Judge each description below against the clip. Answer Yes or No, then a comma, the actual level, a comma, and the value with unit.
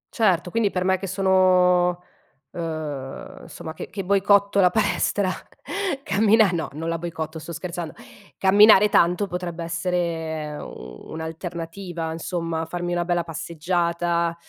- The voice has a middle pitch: Yes, medium, 175 Hz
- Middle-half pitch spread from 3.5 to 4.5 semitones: No, narrow, 2.4 semitones